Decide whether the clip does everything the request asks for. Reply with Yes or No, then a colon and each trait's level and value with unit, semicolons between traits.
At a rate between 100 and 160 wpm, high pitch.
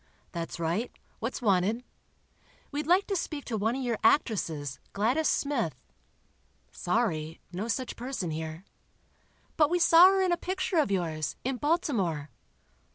Yes: average, 140 wpm; high, 230 Hz